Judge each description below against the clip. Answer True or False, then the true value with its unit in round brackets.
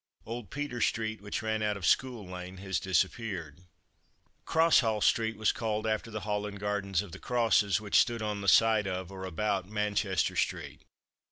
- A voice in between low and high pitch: False (105 Hz)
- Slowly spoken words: False (175 wpm)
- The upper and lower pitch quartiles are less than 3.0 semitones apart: True (2.6 semitones)